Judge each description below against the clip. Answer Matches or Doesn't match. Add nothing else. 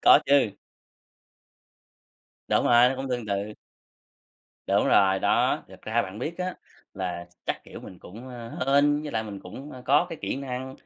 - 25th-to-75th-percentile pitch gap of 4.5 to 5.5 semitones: Matches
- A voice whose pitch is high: Doesn't match